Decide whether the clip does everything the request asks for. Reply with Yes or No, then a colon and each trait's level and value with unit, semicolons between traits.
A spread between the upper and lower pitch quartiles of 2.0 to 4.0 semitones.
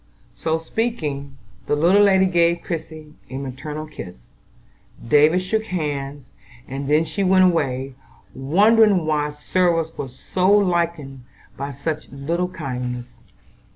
No: average, 4.7 semitones